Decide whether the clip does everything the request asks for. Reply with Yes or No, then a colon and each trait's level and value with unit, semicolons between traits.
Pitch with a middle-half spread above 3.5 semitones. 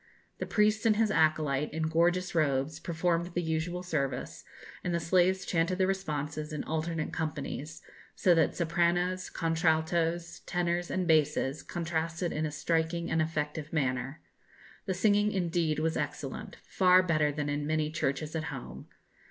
No: narrow, 2.5 semitones